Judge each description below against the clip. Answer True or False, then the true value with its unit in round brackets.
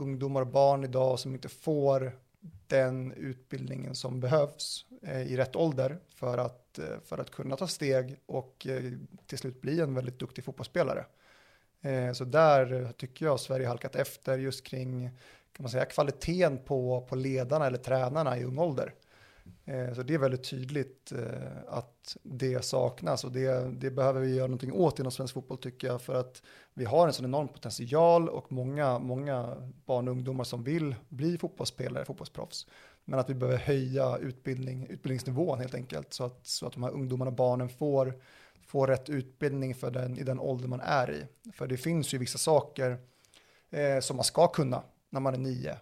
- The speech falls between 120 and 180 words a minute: True (175 wpm)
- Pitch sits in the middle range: False (130 Hz)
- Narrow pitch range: True (1.5 semitones)